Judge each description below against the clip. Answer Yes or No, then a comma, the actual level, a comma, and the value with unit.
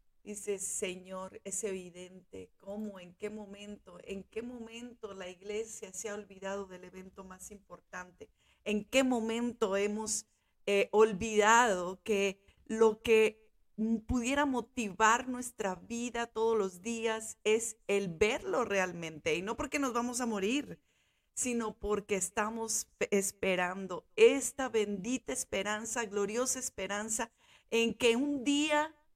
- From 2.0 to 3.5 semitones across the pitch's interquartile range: Yes, average, 2.9 semitones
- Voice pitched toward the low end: No, high, 215 Hz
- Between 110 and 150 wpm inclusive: Yes, slow, 125 wpm